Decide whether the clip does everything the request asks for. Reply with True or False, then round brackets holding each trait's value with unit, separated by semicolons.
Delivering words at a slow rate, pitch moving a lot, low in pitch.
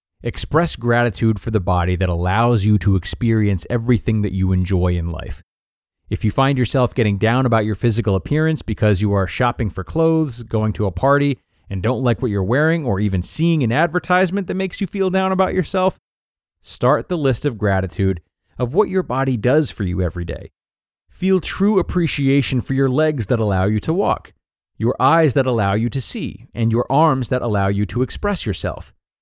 False (195 wpm; 6.5 semitones; 120 Hz)